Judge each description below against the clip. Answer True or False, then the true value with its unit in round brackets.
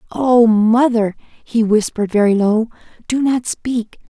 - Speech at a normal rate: False (130 wpm)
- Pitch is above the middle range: True (225 Hz)